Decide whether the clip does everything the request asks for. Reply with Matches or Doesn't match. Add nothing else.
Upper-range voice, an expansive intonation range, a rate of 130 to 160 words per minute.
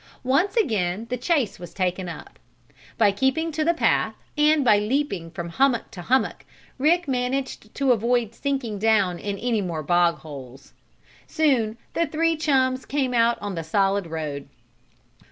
Matches